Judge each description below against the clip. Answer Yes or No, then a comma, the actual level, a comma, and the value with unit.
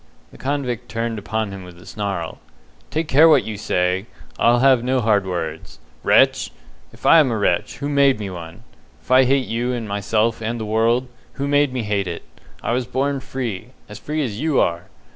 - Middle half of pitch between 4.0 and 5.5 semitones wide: Yes, average, 4.5 semitones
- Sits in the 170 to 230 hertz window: No, low, 115 Hz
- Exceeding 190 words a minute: Yes, average, 200 wpm